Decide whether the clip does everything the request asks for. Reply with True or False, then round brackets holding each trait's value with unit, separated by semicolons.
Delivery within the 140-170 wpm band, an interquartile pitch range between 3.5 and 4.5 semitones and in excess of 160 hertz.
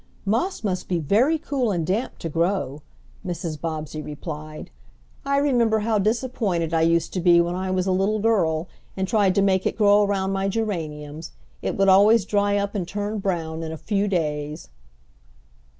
False (180 wpm; 4.1 semitones; 190 Hz)